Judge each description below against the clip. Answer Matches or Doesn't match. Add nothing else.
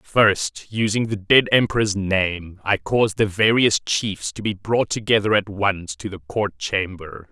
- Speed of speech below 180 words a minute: Matches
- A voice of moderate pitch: Doesn't match